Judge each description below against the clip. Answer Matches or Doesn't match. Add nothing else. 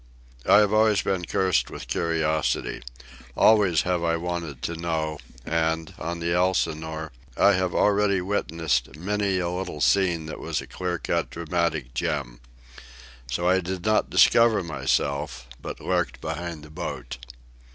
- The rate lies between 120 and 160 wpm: Matches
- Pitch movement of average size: Matches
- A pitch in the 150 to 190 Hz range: Doesn't match